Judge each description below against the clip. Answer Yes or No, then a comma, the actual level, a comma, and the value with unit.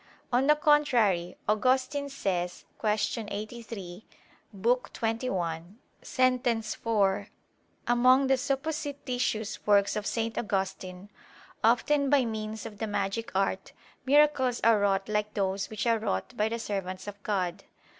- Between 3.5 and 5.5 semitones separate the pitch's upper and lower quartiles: Yes, average, 4.2 semitones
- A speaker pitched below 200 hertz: No, high, 220 Hz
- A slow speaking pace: Yes, slow, 130 wpm